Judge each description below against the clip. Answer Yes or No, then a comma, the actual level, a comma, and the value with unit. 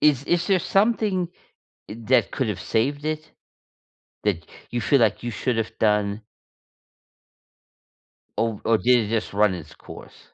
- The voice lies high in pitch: No, low, 115 Hz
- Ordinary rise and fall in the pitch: No, wide, 5.7 semitones